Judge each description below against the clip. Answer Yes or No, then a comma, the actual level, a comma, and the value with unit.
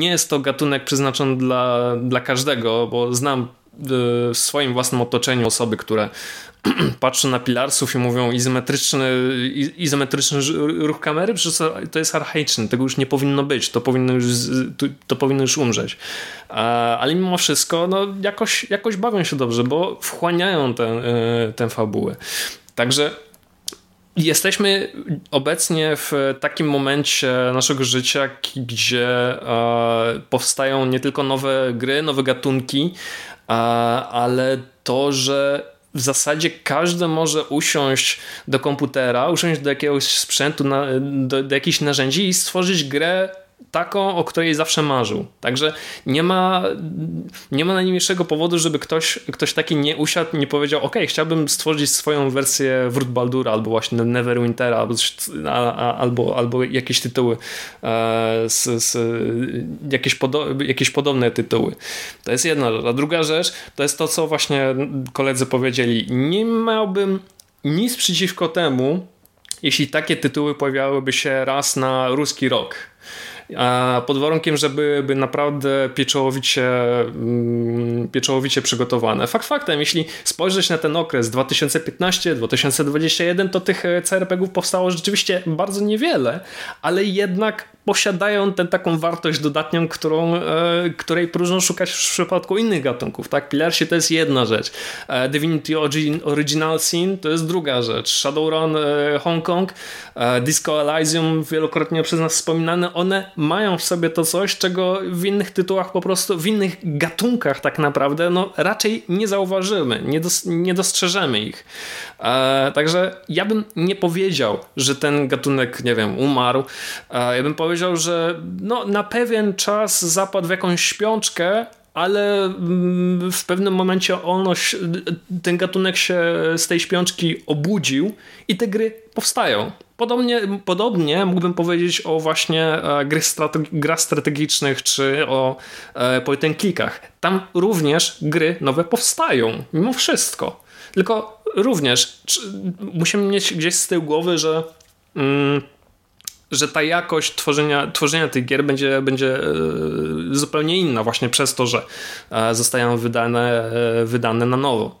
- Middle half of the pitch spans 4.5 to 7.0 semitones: Yes, average, 5.1 semitones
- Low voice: No, medium, 150 Hz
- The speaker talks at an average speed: Yes, average, 135 wpm